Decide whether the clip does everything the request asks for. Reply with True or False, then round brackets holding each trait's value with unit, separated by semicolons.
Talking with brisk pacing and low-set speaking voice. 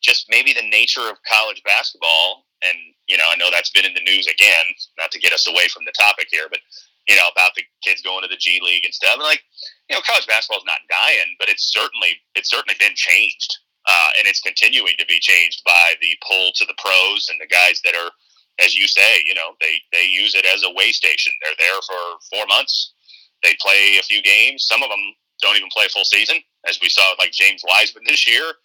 True (240 wpm; 95 Hz)